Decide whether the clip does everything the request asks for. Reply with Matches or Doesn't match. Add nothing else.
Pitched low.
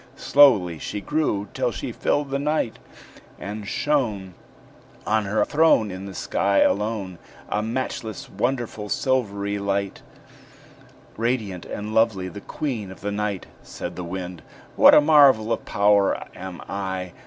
Matches